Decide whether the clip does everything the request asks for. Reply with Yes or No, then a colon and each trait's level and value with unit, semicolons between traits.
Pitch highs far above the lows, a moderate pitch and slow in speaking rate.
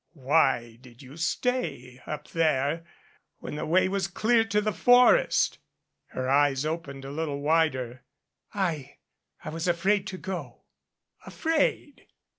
Yes: wide, 5.7 semitones; medium, 160 Hz; slow, 130 wpm